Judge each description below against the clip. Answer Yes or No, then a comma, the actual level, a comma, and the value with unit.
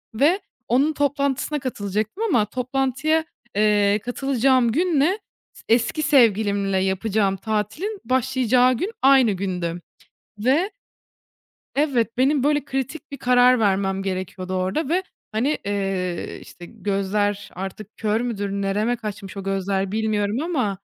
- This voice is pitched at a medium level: No, high, 225 Hz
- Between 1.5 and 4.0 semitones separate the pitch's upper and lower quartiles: No, average, 5.3 semitones